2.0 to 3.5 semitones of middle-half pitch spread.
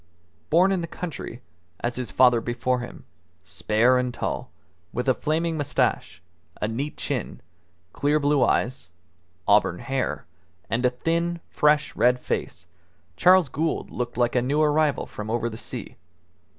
No: average, 4.2 semitones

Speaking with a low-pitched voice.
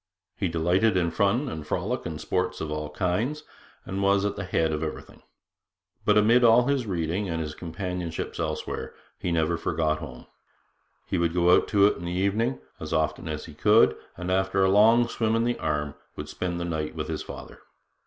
Yes: very low, 90 Hz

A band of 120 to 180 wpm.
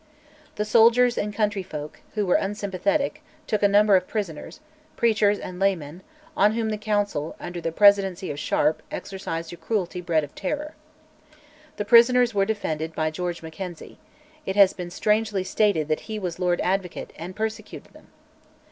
Yes: average, 160 wpm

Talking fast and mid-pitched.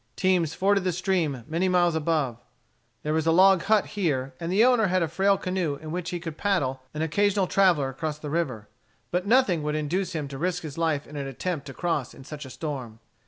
Yes: fast, 220 wpm; medium, 165 Hz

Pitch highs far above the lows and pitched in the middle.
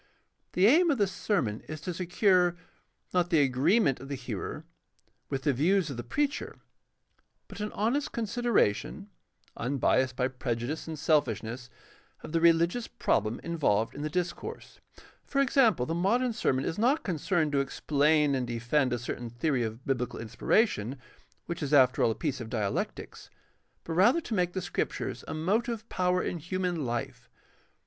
Yes: wide, 6.9 semitones; medium, 155 Hz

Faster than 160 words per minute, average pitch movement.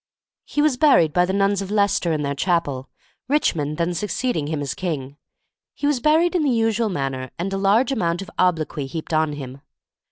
No: average, 195 wpm; wide, 7.0 semitones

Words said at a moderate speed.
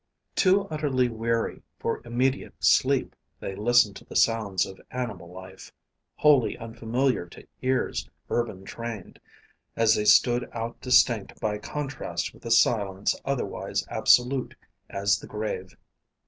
No: slow, 130 wpm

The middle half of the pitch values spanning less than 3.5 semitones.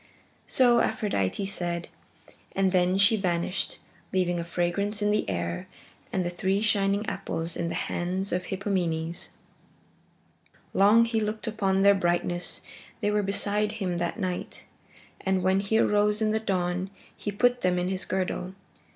Yes: average, 2.8 semitones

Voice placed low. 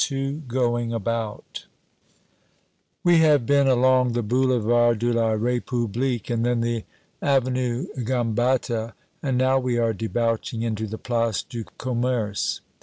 Yes: low, 120 Hz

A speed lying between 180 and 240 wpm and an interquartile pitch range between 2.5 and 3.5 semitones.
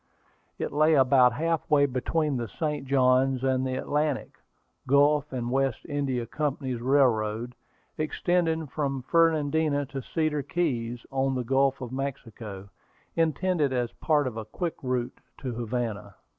No: average, 140 wpm; average, 3.2 semitones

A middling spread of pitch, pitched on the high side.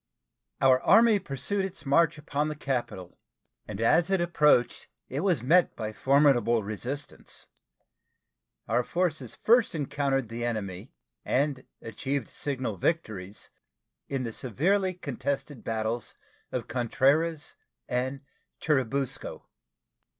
No: average, 4.8 semitones; low, 135 Hz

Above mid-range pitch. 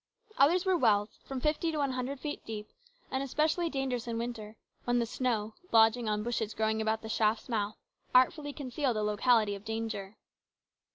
Yes: high, 235 Hz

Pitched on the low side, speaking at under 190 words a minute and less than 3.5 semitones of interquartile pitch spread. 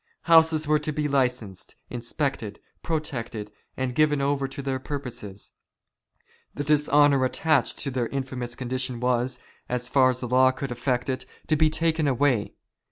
Yes: low, 130 Hz; average, 155 wpm; average, 2.9 semitones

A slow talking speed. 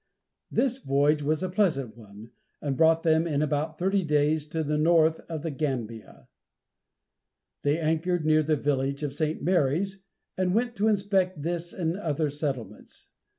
No: average, 155 wpm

